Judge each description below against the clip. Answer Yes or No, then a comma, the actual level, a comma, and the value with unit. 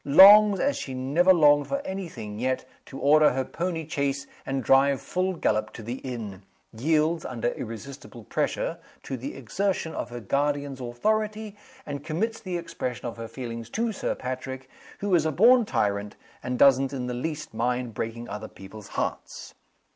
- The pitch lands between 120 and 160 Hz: Yes, low, 135 Hz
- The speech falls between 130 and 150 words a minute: No, average, 175 wpm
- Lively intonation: Yes, wide, 5.7 semitones